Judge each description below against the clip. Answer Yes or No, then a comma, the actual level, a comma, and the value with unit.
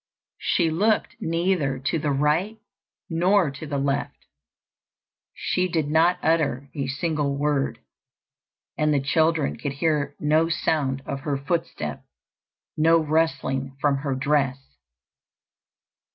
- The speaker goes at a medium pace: No, slow, 120 wpm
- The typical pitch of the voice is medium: Yes, medium, 150 Hz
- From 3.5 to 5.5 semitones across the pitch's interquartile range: No, average, 2.9 semitones